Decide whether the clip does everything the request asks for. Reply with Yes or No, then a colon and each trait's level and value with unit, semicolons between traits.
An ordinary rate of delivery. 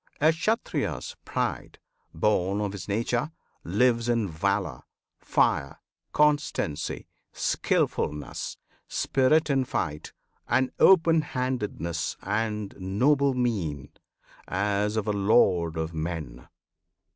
No: slow, 100 wpm